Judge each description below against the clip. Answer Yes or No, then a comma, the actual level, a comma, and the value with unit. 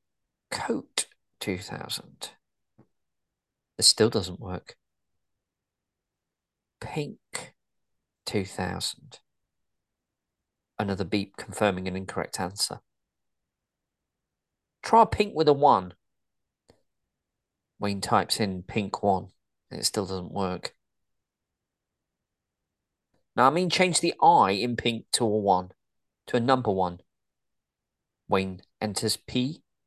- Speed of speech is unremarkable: No, slow, 95 wpm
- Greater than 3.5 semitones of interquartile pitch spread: Yes, average, 4.4 semitones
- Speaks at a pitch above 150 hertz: No, low, 105 Hz